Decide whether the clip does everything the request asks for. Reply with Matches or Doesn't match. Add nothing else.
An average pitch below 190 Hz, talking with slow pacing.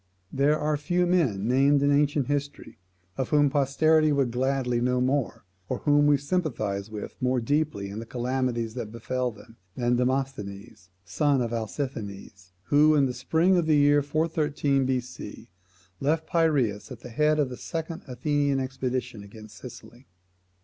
Doesn't match